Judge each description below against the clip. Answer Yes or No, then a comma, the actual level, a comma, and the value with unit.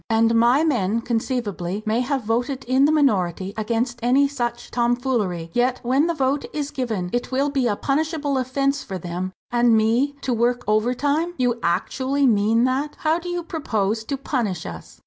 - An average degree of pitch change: Yes, average, 4.0 semitones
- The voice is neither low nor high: No, high, 245 Hz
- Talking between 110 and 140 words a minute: No, average, 175 wpm